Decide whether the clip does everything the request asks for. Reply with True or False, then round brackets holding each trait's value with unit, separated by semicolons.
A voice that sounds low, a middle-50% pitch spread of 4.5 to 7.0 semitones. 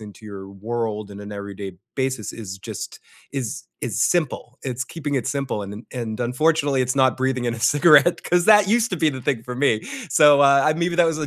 True (130 Hz; 5.3 semitones)